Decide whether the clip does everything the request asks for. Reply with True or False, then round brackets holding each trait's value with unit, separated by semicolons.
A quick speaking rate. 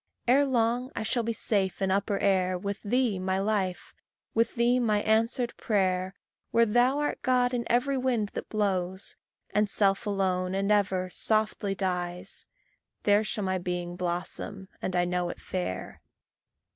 False (160 wpm)